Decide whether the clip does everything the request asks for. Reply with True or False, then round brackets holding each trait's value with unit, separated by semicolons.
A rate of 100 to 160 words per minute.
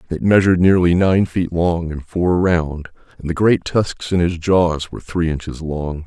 False (200 wpm)